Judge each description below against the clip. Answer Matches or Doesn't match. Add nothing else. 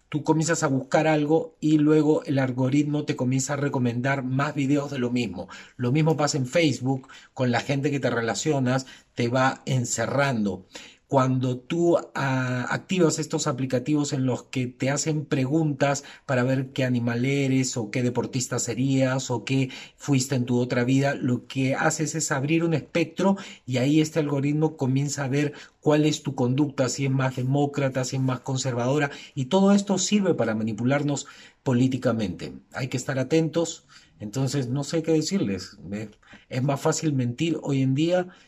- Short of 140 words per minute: Doesn't match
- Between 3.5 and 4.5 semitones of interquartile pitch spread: Doesn't match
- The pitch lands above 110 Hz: Matches